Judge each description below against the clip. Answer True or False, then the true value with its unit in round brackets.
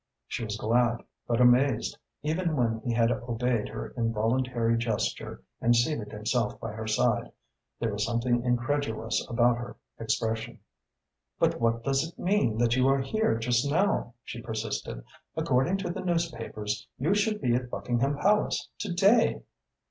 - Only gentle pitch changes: False (3.9 semitones)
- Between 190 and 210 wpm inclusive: False (155 wpm)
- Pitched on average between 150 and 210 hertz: False (120 Hz)